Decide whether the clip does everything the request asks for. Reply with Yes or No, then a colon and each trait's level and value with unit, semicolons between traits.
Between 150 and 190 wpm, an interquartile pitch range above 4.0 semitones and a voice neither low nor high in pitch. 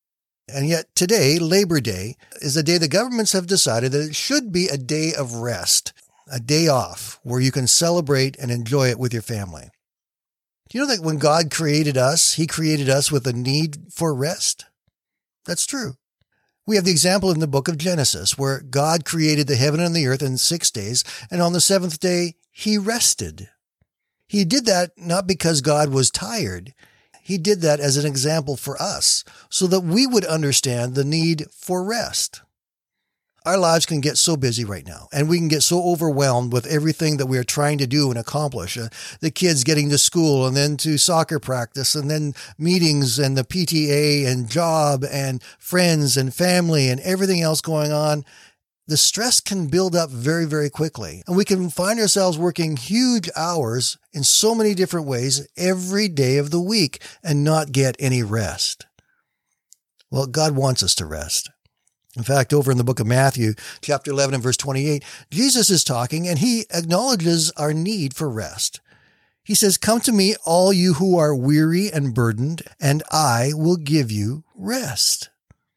Yes: average, 185 wpm; average, 4.5 semitones; medium, 150 Hz